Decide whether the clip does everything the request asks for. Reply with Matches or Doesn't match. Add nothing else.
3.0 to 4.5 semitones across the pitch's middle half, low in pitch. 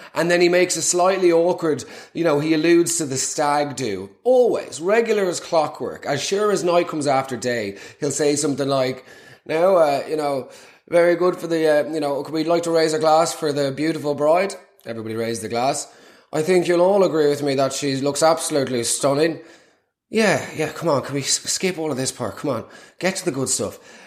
Doesn't match